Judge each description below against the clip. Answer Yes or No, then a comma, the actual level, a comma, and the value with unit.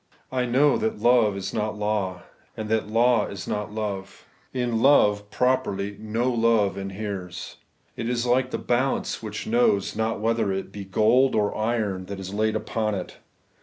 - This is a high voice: No, low, 110 Hz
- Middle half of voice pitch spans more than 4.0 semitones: No, average, 3.1 semitones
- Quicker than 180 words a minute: No, average, 165 wpm